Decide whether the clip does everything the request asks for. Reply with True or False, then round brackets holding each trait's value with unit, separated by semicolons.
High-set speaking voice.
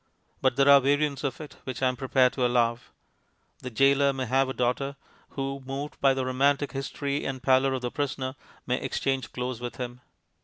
False (135 Hz)